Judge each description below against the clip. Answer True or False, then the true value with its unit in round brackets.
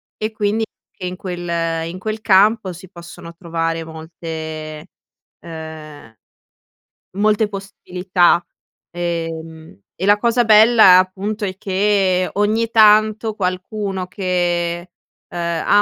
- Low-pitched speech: False (185 Hz)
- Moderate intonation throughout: True (3.7 semitones)